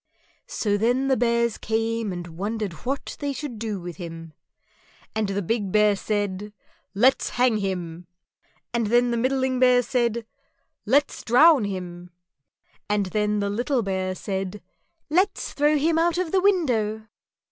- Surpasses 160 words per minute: No, average, 150 wpm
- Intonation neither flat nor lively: Yes, average, 4.5 semitones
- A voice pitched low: No, high, 225 Hz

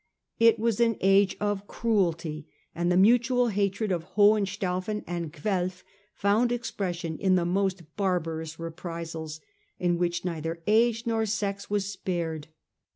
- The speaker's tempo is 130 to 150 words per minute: Yes, slow, 135 wpm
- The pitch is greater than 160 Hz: Yes, high, 190 Hz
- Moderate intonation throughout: Yes, average, 3.8 semitones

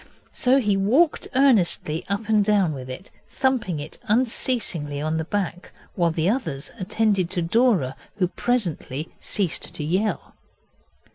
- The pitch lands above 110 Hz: Yes, high, 190 Hz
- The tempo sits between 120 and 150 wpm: Yes, average, 140 wpm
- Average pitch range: No, wide, 5.7 semitones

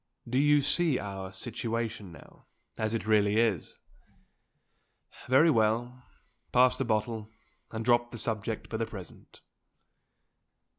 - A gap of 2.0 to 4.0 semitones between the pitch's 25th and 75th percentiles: Yes, narrow, 2.4 semitones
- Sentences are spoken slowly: Yes, slow, 120 wpm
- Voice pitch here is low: Yes, low, 115 Hz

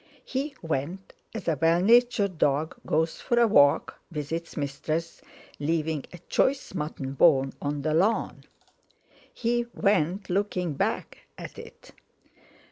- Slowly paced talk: Yes, slow, 130 wpm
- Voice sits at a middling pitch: Yes, medium, 165 Hz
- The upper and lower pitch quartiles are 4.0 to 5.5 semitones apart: Yes, average, 5.2 semitones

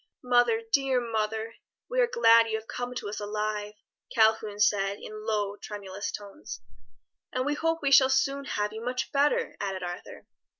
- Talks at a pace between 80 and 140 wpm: No, average, 170 wpm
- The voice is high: Yes, high, 220 Hz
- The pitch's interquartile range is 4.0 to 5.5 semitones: No, average, 3.6 semitones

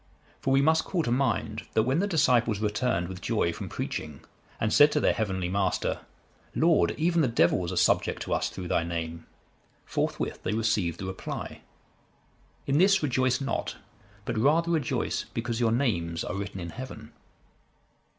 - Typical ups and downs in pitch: No, wide, 6.9 semitones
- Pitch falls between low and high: No, low, 115 Hz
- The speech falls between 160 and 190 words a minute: Yes, average, 170 wpm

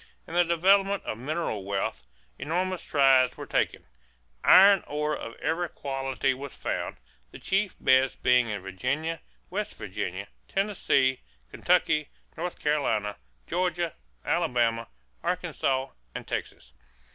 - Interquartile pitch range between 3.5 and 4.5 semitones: No, wide, 5.5 semitones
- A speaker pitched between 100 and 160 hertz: Yes, medium, 140 Hz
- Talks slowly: Yes, slow, 120 wpm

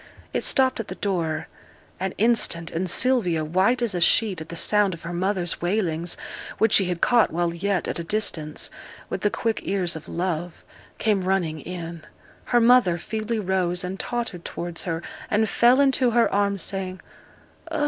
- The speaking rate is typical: Yes, average, 180 wpm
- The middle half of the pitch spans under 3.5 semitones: No, average, 4.3 semitones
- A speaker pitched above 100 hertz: Yes, medium, 185 Hz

